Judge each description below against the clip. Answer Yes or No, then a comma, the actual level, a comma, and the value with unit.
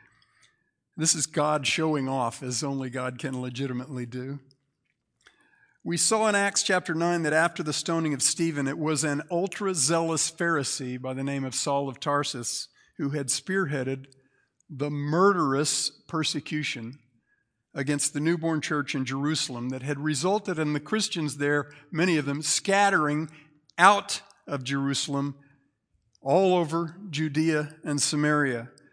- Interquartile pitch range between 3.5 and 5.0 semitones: No, average, 3.0 semitones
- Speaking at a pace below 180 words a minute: Yes, average, 140 wpm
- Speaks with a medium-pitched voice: Yes, medium, 145 Hz